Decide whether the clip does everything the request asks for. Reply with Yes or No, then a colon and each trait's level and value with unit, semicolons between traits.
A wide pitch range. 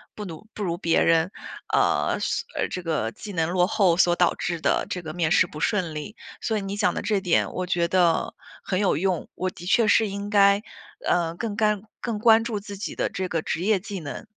No: average, 3.4 semitones